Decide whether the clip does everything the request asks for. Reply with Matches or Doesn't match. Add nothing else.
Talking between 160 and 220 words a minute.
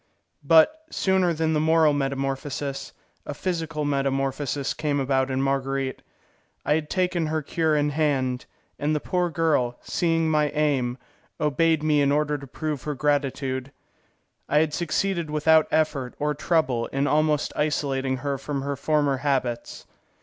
Doesn't match